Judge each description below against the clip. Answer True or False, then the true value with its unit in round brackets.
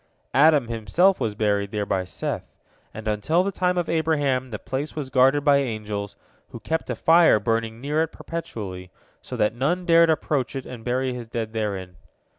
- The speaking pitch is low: True (130 Hz)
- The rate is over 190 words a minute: False (185 wpm)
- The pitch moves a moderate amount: False (6.5 semitones)